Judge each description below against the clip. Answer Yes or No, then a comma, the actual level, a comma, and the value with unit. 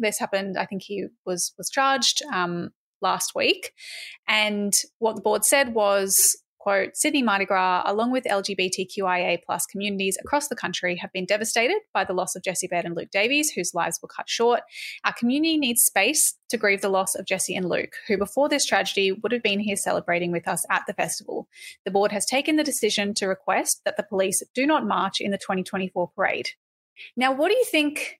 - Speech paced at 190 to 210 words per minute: Yes, average, 200 wpm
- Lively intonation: Yes, wide, 5.9 semitones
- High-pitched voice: Yes, high, 205 Hz